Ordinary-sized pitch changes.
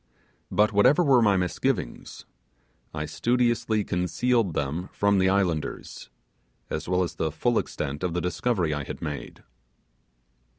No: wide, 6.1 semitones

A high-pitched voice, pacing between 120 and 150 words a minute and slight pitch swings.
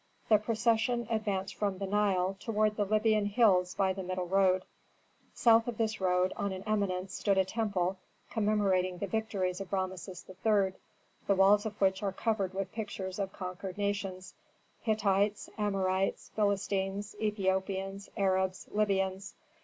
Yes: high, 195 Hz; average, 145 wpm; narrow, 2.0 semitones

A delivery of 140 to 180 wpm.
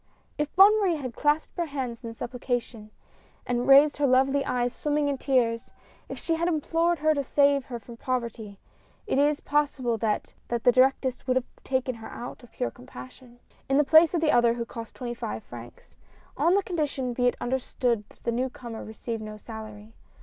No: average, 200 wpm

